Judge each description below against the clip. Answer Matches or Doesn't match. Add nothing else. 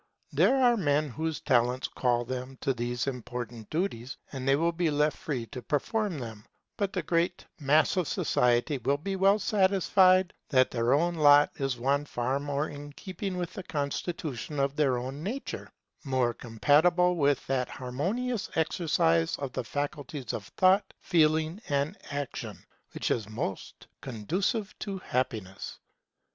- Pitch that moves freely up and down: Matches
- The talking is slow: Doesn't match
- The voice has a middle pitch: Matches